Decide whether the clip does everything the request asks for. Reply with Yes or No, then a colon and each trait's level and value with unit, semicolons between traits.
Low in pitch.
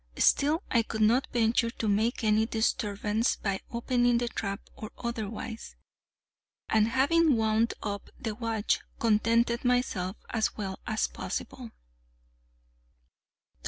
No: high, 225 Hz